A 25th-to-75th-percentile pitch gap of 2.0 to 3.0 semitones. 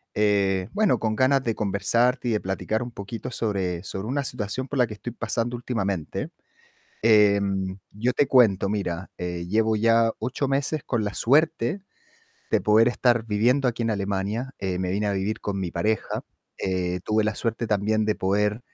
No: average, 3.5 semitones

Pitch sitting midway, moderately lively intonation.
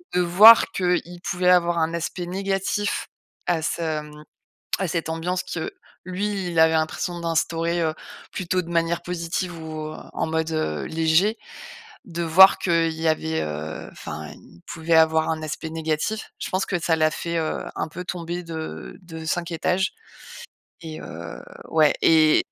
No: medium, 165 Hz; narrow, 1.9 semitones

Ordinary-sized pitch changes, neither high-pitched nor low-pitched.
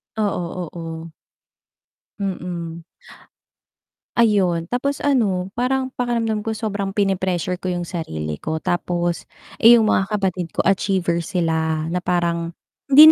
Yes: average, 4.1 semitones; medium, 180 Hz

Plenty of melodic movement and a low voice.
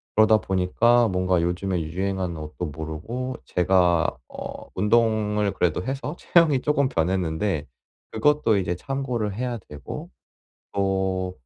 No: average, 5.0 semitones; very low, 95 Hz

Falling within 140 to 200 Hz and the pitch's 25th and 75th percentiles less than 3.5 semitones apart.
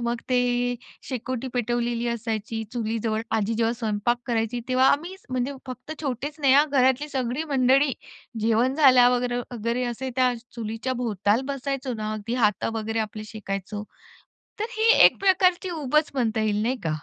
No: high, 245 Hz; average, 2.8 semitones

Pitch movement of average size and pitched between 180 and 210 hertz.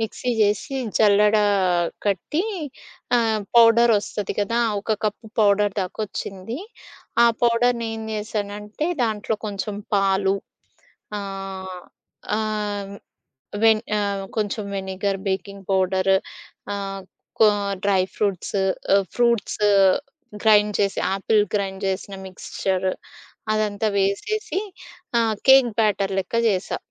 No: narrow, 2.1 semitones; high, 205 Hz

